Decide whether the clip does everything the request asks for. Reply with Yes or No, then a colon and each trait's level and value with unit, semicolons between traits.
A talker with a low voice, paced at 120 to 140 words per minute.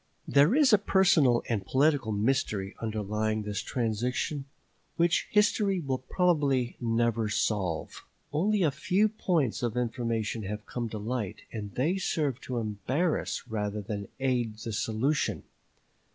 Yes: low, 120 Hz; slow, 135 wpm